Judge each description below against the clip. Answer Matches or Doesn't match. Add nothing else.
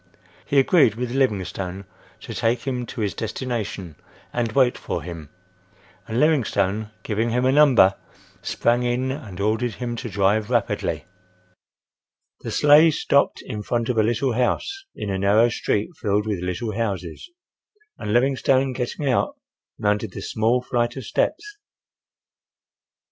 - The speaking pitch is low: Matches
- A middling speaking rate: Matches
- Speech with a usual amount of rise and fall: Matches